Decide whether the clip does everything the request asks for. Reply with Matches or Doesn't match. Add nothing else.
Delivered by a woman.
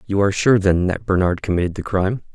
Doesn't match